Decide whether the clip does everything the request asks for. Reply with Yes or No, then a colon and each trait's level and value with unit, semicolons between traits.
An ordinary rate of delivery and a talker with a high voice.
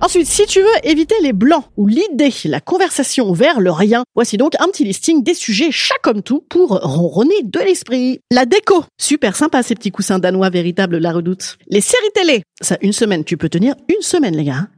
Yes: average, 210 wpm; very high, 255 Hz